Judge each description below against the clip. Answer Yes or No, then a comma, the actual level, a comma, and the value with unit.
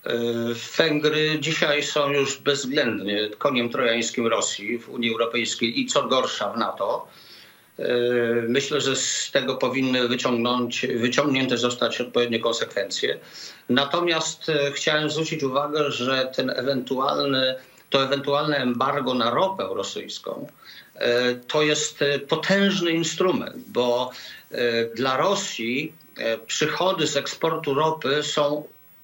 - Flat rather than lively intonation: No, average, 3.8 semitones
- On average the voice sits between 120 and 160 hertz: Yes, low, 135 Hz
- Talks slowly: Yes, slow, 105 wpm